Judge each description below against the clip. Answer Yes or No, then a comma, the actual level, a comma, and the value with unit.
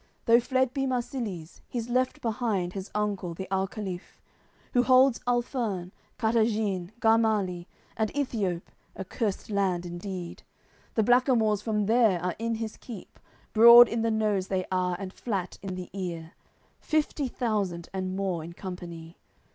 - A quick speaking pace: No, average, 145 wpm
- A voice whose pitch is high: Yes, high, 210 Hz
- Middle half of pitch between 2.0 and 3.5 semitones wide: No, average, 4.3 semitones